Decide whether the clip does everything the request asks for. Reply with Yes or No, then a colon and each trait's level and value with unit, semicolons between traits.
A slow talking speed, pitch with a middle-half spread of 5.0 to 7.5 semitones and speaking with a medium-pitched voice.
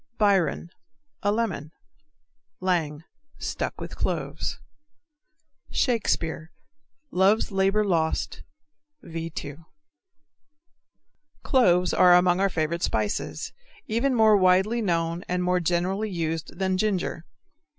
No: slow, 100 wpm; average, 3.5 semitones; medium, 180 Hz